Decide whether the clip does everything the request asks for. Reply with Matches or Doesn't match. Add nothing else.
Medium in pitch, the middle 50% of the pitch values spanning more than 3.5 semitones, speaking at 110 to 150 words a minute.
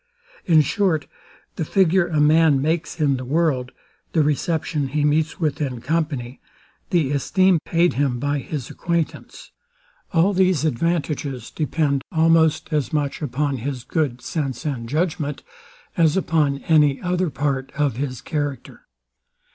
Doesn't match